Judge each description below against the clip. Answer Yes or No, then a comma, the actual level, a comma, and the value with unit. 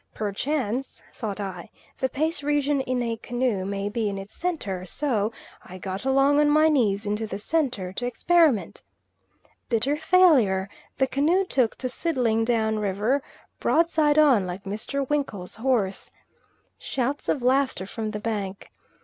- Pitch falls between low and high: No, high, 240 Hz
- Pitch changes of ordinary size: No, wide, 5.9 semitones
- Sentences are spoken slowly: No, average, 150 wpm